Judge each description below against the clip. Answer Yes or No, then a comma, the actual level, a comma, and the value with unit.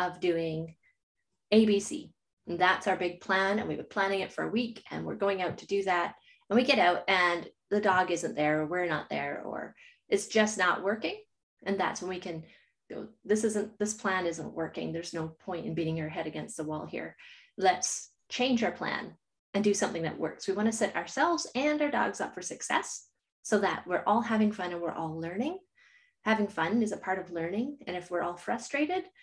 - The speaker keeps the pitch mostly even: No, average, 4.8 semitones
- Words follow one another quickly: Yes, fast, 220 wpm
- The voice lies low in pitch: No, high, 195 Hz